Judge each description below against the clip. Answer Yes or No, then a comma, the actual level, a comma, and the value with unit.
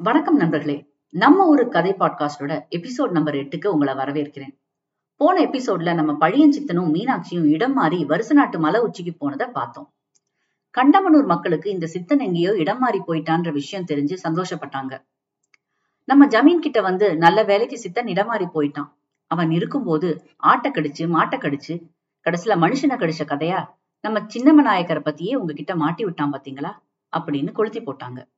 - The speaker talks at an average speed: No, fast, 145 wpm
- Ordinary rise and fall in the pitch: No, wide, 6.3 semitones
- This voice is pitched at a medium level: Yes, medium, 170 Hz